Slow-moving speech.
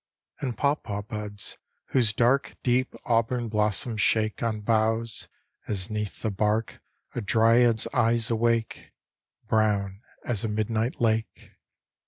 Yes: slow, 125 wpm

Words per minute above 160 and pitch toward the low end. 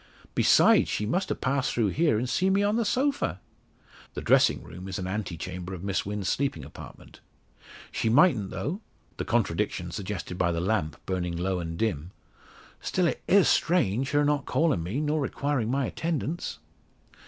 Yes: average, 175 wpm; low, 110 Hz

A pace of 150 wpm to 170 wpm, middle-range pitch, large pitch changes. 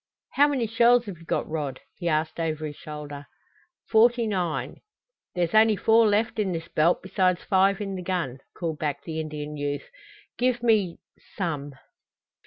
Yes: average, 165 wpm; medium, 180 Hz; wide, 6.0 semitones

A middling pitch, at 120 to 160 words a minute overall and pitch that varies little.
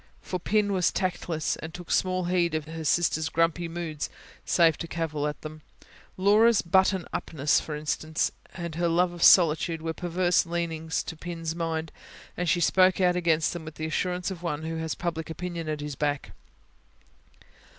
No: medium, 165 Hz; average, 175 wpm; narrow, 2.0 semitones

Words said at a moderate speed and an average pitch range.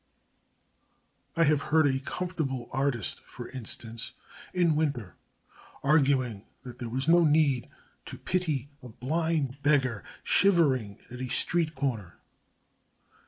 No: slow, 120 wpm; average, 4.3 semitones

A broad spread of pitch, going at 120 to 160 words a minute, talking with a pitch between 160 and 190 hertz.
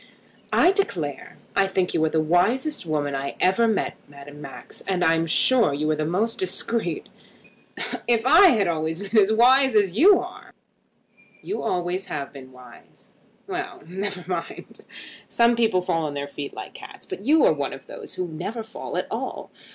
No: wide, 6.8 semitones; average, 180 wpm; medium, 185 Hz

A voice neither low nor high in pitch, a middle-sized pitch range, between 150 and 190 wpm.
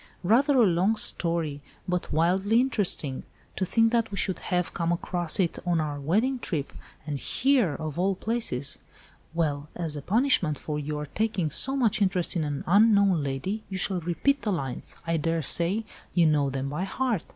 No: medium, 175 Hz; wide, 5.8 semitones; average, 175 wpm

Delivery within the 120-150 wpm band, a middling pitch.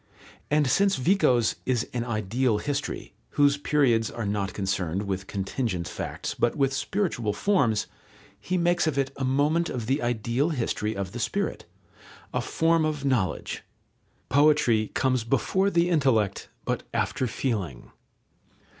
No: average, 140 wpm; low, 130 Hz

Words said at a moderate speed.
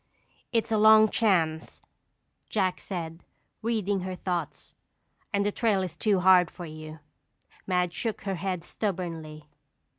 No: slow, 130 wpm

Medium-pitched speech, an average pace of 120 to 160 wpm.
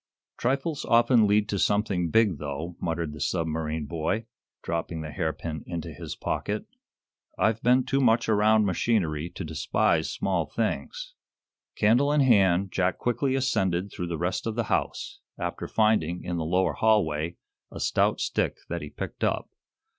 No: very low, 95 Hz; average, 155 wpm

